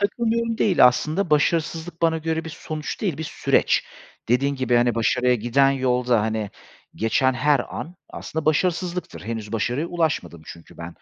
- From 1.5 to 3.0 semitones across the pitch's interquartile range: No, wide, 5.5 semitones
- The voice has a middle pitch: Yes, medium, 145 Hz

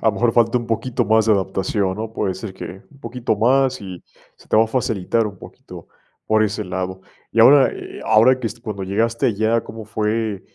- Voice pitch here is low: Yes, low, 110 Hz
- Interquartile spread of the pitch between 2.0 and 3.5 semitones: Yes, narrow, 2.6 semitones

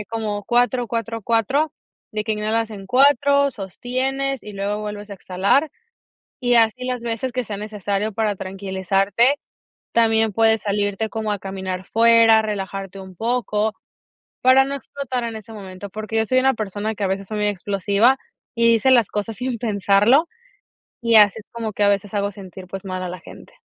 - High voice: Yes, high, 215 Hz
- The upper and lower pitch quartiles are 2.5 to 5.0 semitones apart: Yes, average, 2.8 semitones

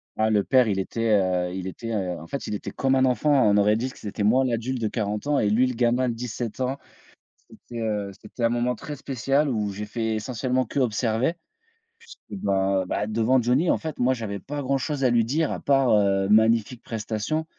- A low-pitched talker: Yes, low, 115 Hz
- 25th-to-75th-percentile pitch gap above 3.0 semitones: Yes, average, 3.7 semitones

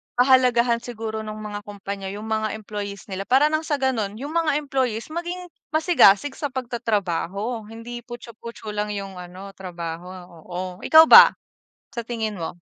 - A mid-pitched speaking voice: No, high, 220 Hz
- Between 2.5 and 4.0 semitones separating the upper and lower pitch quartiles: No, average, 4.6 semitones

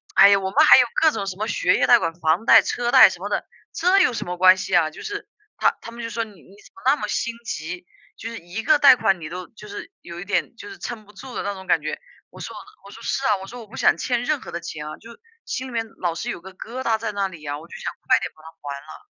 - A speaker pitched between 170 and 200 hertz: No, high, 210 Hz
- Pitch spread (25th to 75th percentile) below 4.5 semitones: No, average, 5.1 semitones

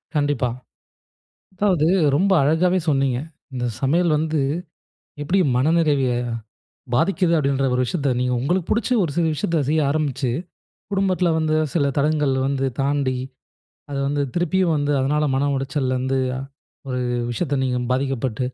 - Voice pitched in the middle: Yes, medium, 145 Hz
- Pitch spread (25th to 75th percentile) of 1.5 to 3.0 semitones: No, average, 3.7 semitones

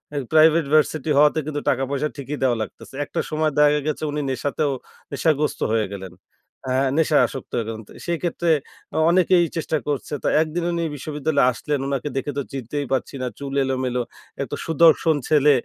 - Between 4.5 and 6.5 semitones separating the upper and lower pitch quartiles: No, average, 2.8 semitones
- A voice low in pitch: No, medium, 145 Hz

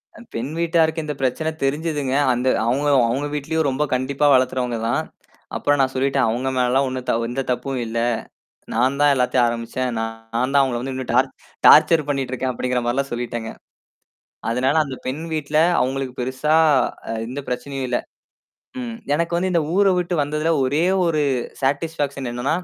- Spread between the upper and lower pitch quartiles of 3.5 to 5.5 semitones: No, average, 2.9 semitones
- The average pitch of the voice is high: No, low, 135 Hz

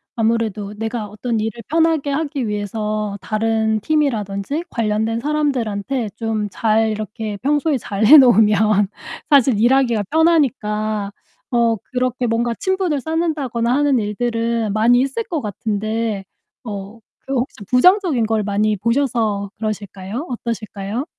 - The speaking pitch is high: Yes, high, 230 Hz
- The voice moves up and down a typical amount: Yes, average, 4.1 semitones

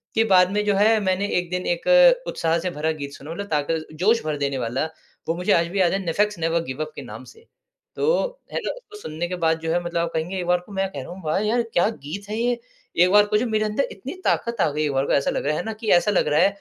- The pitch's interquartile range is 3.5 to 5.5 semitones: Yes, average, 4.8 semitones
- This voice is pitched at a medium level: Yes, medium, 180 Hz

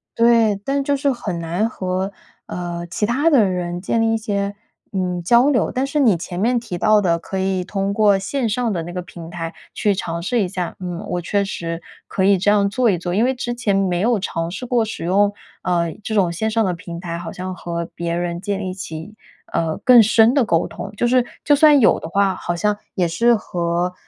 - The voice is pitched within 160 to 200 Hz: Yes, high, 195 Hz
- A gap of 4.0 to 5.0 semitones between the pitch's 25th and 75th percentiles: Yes, average, 4.5 semitones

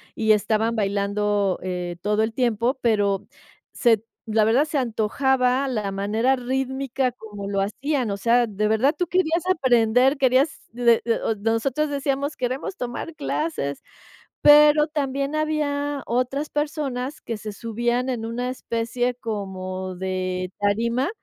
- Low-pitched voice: No, high, 240 Hz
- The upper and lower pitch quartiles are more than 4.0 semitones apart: Yes, average, 4.5 semitones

